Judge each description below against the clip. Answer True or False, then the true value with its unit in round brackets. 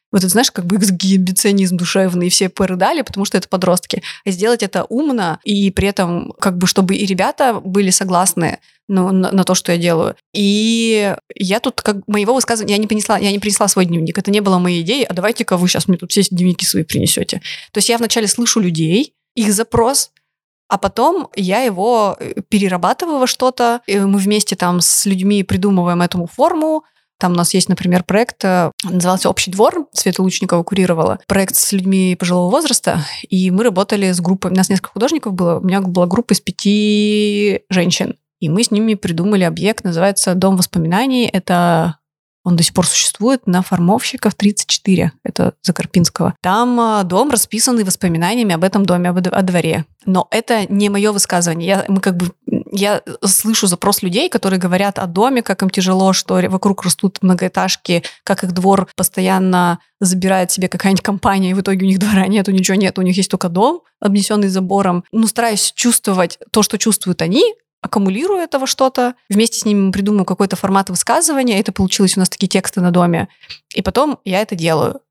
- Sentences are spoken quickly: True (185 wpm)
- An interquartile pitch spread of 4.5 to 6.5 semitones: False (2.5 semitones)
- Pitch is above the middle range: True (195 Hz)